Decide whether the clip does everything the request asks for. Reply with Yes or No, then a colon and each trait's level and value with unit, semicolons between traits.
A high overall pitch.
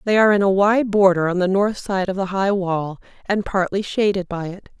Yes: high, 195 Hz